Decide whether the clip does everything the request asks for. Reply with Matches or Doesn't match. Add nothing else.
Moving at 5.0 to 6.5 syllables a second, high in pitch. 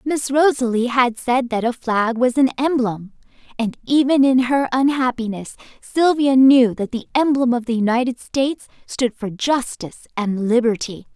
Doesn't match